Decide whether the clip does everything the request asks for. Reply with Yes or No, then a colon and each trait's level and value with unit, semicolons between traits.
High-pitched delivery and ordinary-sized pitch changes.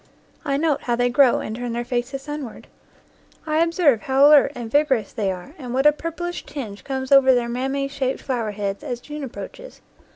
Yes: very high, 265 Hz; average, 3.4 semitones